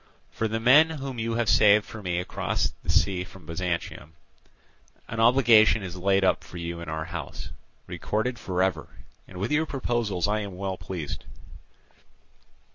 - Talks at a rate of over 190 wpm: No, average, 160 wpm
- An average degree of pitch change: Yes, average, 4.2 semitones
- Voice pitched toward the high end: No, low, 100 Hz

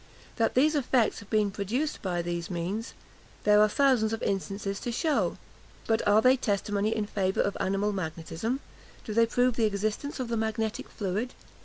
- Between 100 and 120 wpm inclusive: No, average, 175 wpm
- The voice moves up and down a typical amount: Yes, average, 3.0 semitones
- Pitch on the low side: No, high, 215 Hz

